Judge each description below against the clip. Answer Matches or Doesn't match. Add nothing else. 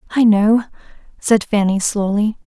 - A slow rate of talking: Matches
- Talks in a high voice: Matches